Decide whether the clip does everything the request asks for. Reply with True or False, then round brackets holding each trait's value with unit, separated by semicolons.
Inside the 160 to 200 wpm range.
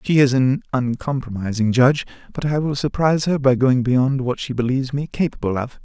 True (195 wpm)